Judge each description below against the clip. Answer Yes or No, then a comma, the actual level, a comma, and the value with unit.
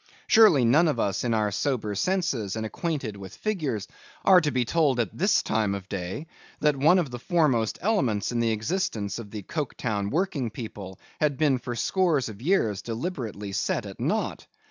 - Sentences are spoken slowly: No, average, 185 wpm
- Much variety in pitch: Yes, wide, 7.0 semitones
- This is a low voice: Yes, low, 125 Hz